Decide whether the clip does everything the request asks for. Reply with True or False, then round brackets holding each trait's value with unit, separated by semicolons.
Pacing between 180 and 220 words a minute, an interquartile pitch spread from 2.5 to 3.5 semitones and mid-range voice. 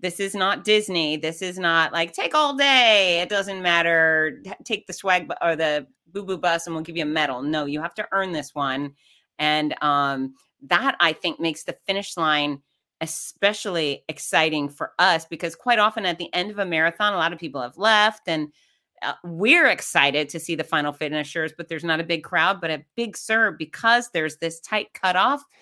False (205 wpm; 3.9 semitones; 170 Hz)